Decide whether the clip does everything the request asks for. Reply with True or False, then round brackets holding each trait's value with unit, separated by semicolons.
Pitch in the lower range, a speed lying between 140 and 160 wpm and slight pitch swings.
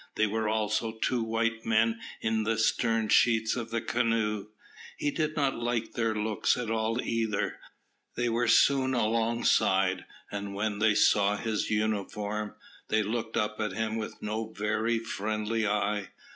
True (110 Hz; 155 wpm; 1.4 semitones)